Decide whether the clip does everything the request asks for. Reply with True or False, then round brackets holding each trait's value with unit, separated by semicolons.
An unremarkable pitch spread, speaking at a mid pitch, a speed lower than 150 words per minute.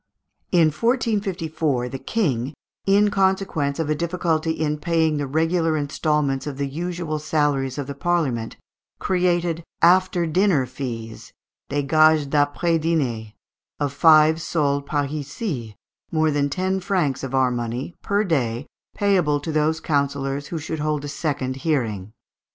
True (3.5 semitones; 150 Hz; 140 wpm)